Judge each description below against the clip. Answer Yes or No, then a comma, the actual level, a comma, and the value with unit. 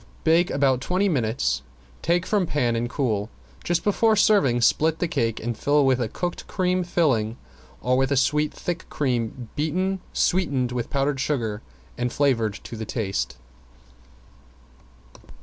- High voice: No, low, 135 Hz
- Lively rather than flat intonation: Yes, wide, 6.4 semitones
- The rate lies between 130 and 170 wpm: Yes, average, 145 wpm